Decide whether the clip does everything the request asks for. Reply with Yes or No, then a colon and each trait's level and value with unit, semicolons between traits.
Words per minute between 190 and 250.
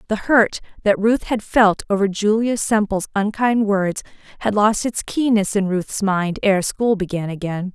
No: average, 170 wpm